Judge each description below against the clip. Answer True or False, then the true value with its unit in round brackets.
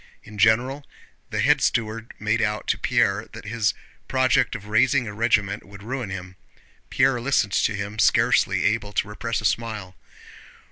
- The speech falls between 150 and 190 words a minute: True (160 wpm)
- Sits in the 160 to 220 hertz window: False (110 Hz)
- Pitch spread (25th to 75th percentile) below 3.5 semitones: True (2.4 semitones)